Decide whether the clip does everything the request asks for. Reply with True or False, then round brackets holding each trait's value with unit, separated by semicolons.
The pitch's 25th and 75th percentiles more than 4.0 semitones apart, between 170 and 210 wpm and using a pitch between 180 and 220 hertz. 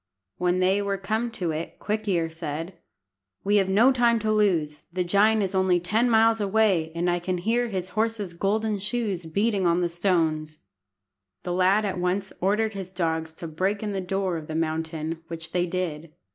False (3.7 semitones; 190 wpm; 185 Hz)